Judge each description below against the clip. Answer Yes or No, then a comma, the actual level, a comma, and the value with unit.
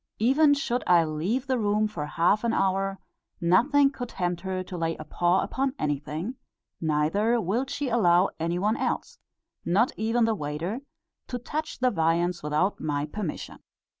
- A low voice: No, high, 195 Hz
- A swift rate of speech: No, average, 165 wpm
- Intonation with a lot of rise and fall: Yes, wide, 6.1 semitones